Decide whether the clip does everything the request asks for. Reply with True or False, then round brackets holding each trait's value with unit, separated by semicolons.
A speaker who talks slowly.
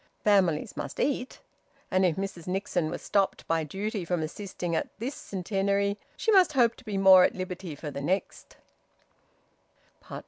False (160 wpm)